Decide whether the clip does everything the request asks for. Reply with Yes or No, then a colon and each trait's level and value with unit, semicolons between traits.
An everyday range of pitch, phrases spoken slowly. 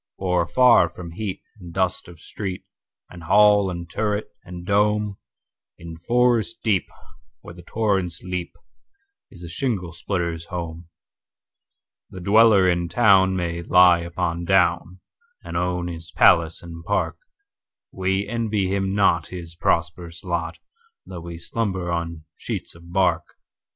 Yes: average, 3.2 semitones; slow, 120 wpm